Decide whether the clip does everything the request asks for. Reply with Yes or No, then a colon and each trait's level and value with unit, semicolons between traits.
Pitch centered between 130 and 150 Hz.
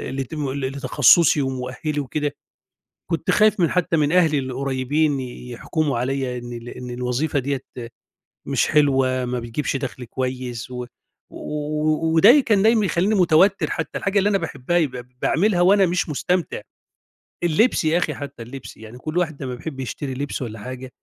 Yes: medium, 140 Hz